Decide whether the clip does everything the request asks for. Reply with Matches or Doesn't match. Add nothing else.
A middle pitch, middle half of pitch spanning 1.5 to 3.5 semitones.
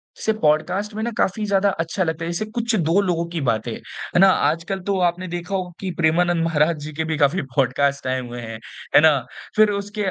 Doesn't match